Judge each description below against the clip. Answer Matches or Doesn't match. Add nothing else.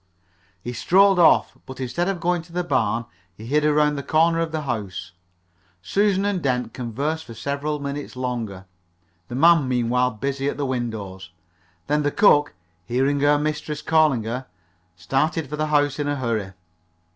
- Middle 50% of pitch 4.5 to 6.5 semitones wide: Doesn't match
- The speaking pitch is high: Doesn't match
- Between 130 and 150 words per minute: Doesn't match